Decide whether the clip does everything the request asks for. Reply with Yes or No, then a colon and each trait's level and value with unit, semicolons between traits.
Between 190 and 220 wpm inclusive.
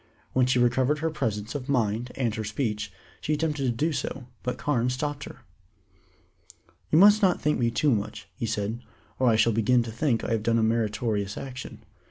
Yes: average, 200 wpm